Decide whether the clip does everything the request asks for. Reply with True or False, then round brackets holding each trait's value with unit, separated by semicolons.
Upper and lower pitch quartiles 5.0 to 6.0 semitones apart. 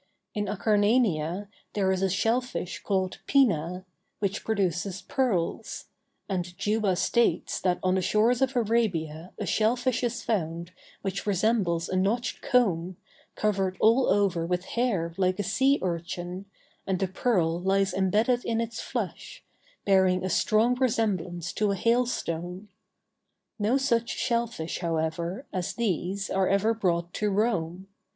False (4.1 semitones)